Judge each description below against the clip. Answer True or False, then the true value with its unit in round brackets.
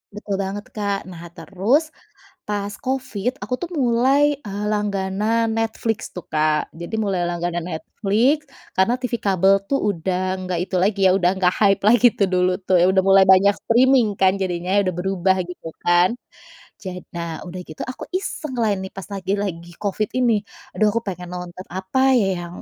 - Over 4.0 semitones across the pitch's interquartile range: False (3.4 semitones)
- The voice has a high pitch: True (195 Hz)